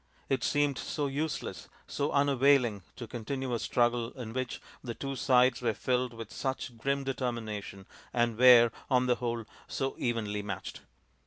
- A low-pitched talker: Yes, low, 125 Hz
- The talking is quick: No, average, 155 wpm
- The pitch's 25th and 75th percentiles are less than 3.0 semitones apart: Yes, narrow, 2.6 semitones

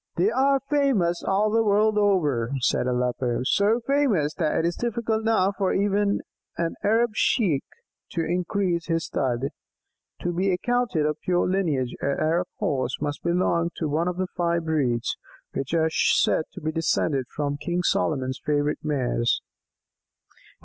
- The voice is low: No, medium, 170 Hz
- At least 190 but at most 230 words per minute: No, average, 155 wpm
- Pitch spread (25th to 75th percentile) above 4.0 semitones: Yes, wide, 5.5 semitones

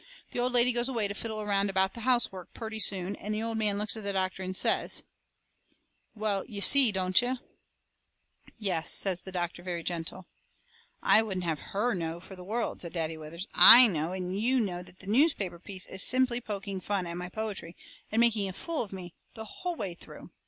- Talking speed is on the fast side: Yes, fast, 210 wpm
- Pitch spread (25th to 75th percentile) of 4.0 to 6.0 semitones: No, average, 3.5 semitones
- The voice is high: Yes, high, 200 Hz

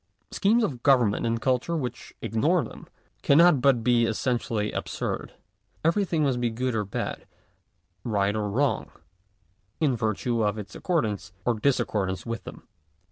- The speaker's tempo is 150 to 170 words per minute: No, average, 140 wpm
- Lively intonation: No, average, 4.4 semitones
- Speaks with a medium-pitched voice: No, low, 120 Hz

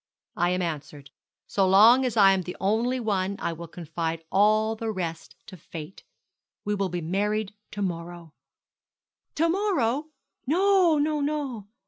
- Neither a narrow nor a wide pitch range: No, wide, 6.1 semitones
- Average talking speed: Yes, average, 150 wpm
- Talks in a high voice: Yes, high, 200 Hz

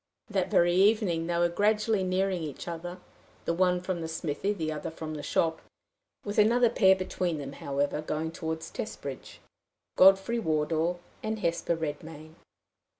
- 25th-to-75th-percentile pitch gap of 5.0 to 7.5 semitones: No, average, 3.3 semitones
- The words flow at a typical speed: Yes, average, 150 wpm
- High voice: No, medium, 170 Hz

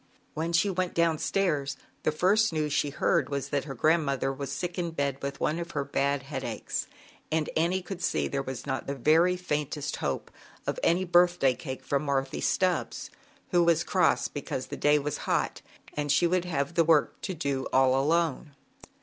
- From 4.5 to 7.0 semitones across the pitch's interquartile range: No, average, 3.6 semitones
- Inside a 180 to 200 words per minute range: Yes, average, 185 wpm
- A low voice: No, medium, 150 Hz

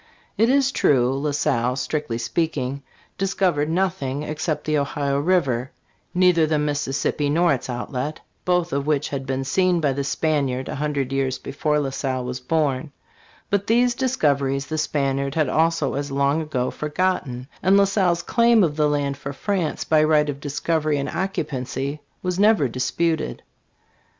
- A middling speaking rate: Yes, average, 160 wpm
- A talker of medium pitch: Yes, medium, 150 Hz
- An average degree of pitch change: Yes, average, 3.7 semitones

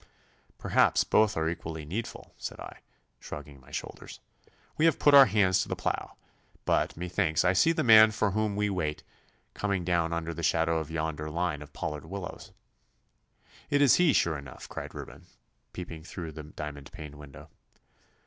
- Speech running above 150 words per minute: Yes, average, 170 wpm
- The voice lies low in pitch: Yes, very low, 85 Hz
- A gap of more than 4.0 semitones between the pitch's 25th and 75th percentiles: Yes, average, 4.8 semitones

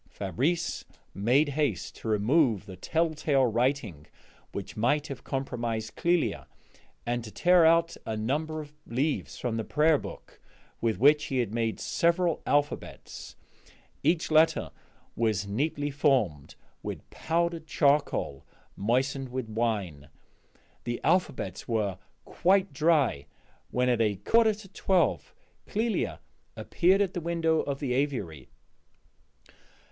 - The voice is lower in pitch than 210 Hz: Yes, low, 135 Hz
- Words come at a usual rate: No, slow, 120 wpm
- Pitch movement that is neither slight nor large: No, wide, 6.3 semitones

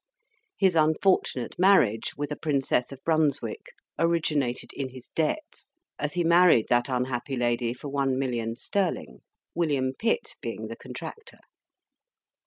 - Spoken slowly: Yes, slow, 130 wpm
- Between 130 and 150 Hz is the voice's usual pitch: Yes, medium, 140 Hz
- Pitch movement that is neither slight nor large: Yes, average, 5.0 semitones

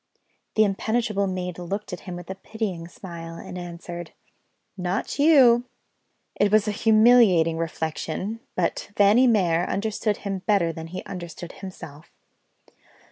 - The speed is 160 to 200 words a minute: No, slow, 135 wpm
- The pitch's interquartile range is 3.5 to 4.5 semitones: Yes, average, 3.9 semitones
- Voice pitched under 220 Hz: Yes, high, 190 Hz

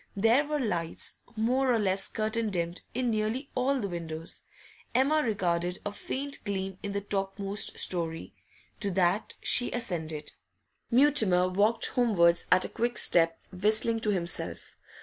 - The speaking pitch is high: Yes, high, 205 Hz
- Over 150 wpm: No, average, 145 wpm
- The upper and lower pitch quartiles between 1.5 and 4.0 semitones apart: No, average, 4.6 semitones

